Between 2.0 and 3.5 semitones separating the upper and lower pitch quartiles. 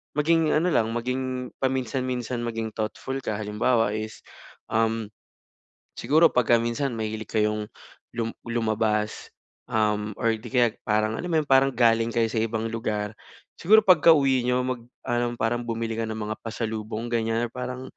Yes: narrow, 2.5 semitones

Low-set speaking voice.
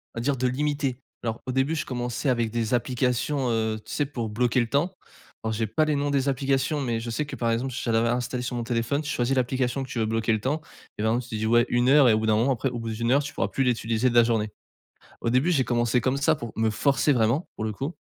Yes: low, 125 Hz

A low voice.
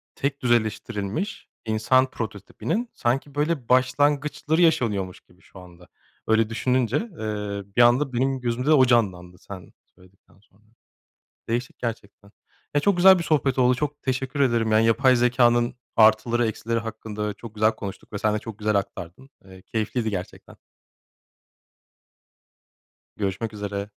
Yes: low, 115 Hz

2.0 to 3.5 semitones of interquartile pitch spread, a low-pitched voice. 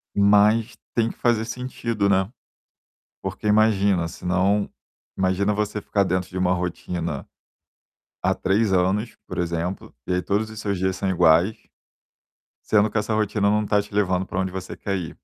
Yes: narrow, 2.5 semitones; low, 100 Hz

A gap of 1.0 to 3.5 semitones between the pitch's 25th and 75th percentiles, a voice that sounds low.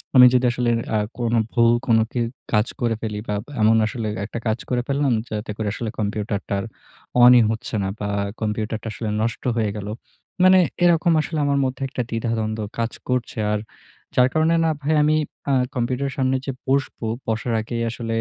Yes: average, 2.9 semitones; low, 115 Hz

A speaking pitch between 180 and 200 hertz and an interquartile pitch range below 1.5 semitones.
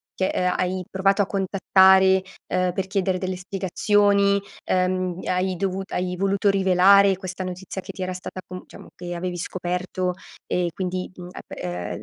Yes: medium, 185 Hz; narrow, 1.0 semitones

